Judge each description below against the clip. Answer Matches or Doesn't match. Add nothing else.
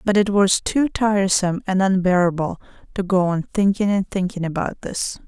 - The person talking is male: Doesn't match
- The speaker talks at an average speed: Matches